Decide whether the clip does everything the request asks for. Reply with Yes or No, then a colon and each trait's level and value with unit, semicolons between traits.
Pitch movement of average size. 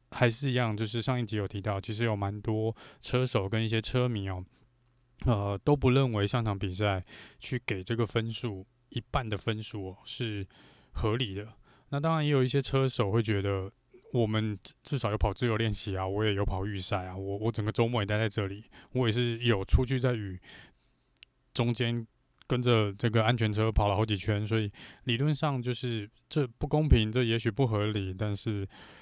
Yes: average, 3.2 semitones